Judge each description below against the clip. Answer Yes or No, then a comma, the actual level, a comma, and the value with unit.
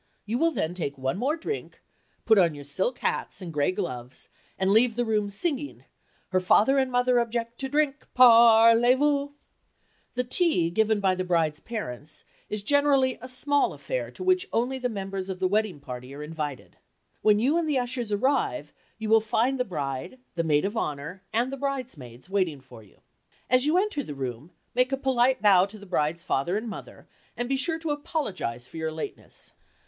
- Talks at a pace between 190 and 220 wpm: Yes, average, 195 wpm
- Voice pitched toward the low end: No, high, 220 Hz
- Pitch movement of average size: No, wide, 7.7 semitones